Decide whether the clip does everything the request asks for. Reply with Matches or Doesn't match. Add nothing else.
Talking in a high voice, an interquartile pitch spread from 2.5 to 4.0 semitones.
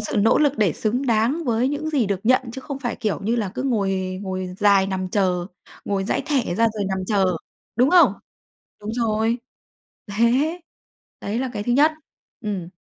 Doesn't match